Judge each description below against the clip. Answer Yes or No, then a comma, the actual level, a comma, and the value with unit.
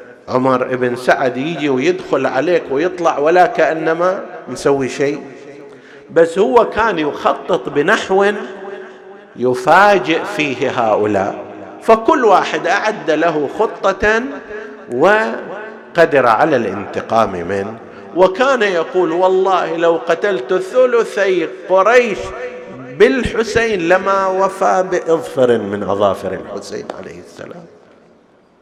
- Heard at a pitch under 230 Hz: Yes, medium, 185 Hz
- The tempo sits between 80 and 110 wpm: Yes, average, 90 wpm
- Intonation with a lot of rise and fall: Yes, wide, 7.5 semitones